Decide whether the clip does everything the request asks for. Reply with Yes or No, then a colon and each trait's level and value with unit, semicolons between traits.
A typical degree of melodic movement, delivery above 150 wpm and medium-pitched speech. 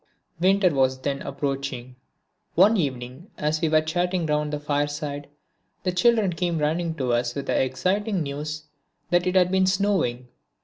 Yes: average, 4.6 semitones; average, 160 wpm; medium, 155 Hz